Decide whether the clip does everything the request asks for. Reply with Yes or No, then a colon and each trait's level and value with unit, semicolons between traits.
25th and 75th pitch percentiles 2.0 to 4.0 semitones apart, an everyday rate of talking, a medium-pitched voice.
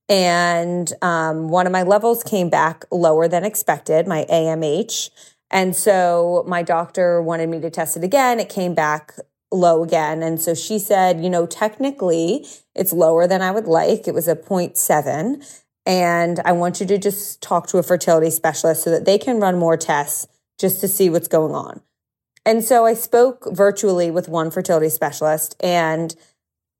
Yes: average, 2.9 semitones; average, 175 wpm; medium, 175 Hz